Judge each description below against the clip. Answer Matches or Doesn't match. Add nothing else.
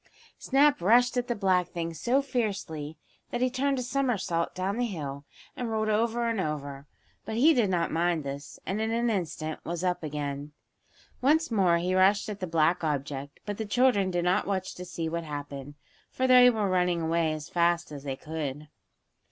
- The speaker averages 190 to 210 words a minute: Matches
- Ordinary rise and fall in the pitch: Doesn't match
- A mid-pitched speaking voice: Matches